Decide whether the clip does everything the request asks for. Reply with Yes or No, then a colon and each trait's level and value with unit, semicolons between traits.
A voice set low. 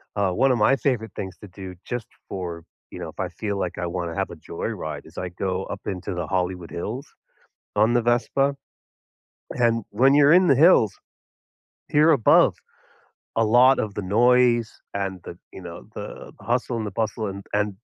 Yes: low, 105 Hz